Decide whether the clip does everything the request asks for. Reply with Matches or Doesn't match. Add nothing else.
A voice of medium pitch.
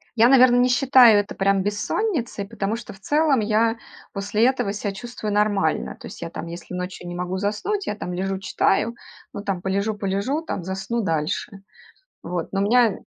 Doesn't match